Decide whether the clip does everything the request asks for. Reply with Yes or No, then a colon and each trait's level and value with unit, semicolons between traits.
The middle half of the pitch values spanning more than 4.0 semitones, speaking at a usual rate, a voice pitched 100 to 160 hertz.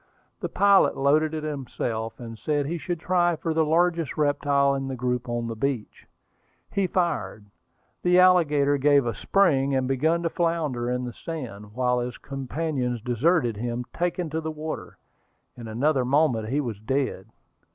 Yes: average, 4.7 semitones; average, 165 wpm; medium, 140 Hz